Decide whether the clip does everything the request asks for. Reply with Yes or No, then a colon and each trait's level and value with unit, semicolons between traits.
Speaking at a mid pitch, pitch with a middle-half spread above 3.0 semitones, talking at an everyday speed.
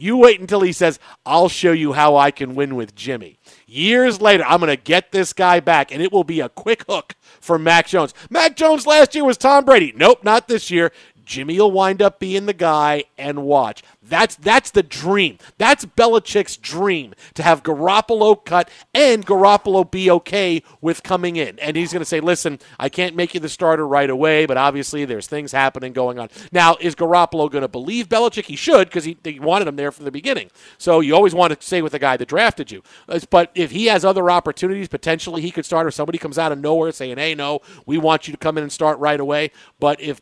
No: medium, 170 Hz; average, 4.6 semitones; fast, 225 wpm